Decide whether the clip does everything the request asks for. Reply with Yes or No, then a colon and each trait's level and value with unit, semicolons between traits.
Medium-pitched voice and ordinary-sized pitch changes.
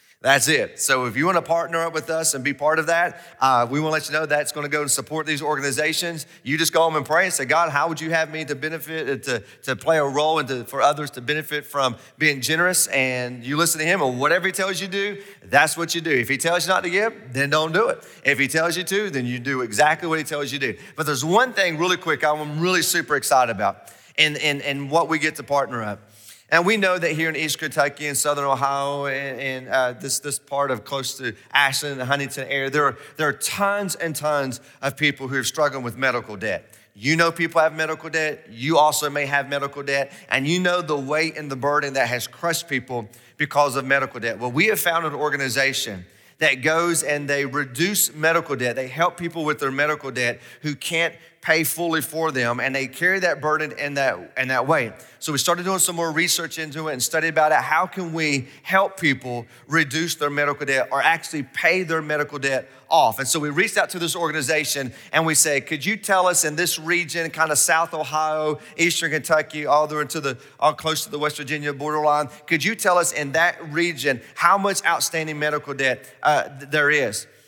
Yes: medium, 150 Hz; average, 3.1 semitones